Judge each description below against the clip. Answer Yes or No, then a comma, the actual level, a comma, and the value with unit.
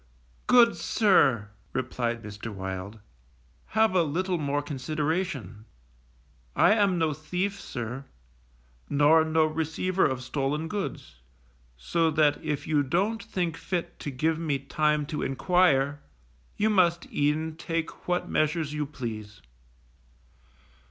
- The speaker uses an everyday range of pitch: Yes, average, 4.4 semitones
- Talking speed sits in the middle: No, slow, 120 wpm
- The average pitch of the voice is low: No, medium, 155 Hz